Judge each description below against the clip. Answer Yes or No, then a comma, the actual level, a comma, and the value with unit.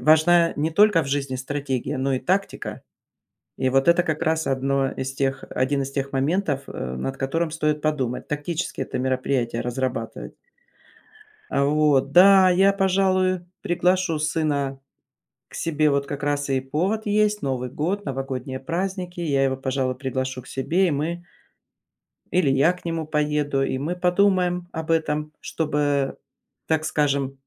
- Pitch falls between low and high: Yes, medium, 150 Hz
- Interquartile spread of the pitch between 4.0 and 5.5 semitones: Yes, average, 4.3 semitones